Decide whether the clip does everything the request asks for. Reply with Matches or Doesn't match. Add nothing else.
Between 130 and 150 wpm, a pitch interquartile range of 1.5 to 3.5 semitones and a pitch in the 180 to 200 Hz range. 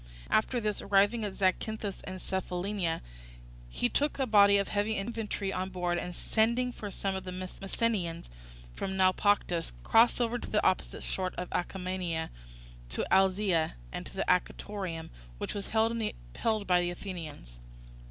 Matches